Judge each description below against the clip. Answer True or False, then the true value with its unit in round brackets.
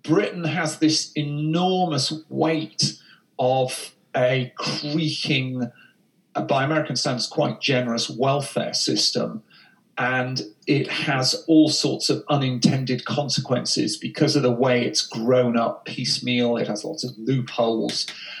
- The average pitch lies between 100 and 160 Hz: True (135 Hz)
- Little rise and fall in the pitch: False (3.6 semitones)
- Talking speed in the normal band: False (115 wpm)